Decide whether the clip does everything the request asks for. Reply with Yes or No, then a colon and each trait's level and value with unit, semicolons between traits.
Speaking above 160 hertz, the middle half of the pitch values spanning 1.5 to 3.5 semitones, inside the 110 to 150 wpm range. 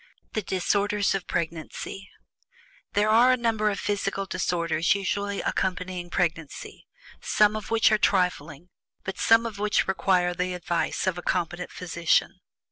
Yes: high, 190 Hz; average, 2.8 semitones; average, 140 wpm